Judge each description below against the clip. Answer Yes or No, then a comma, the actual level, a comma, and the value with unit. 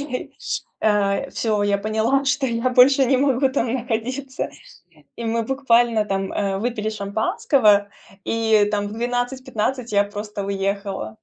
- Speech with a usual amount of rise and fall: Yes, average, 3.8 semitones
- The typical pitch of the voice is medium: No, high, 225 Hz